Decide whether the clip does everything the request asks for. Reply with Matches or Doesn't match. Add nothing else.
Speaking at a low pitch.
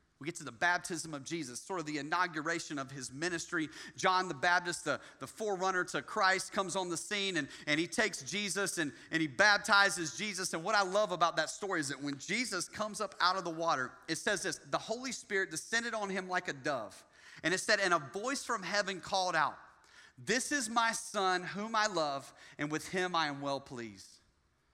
Doesn't match